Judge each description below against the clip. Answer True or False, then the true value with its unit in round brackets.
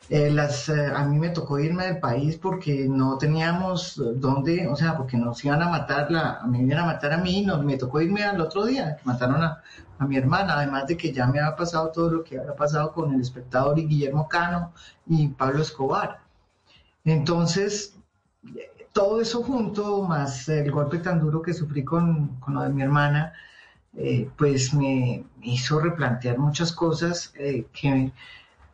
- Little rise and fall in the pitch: False (3.7 semitones)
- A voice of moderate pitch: True (150 Hz)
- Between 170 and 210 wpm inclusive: True (190 wpm)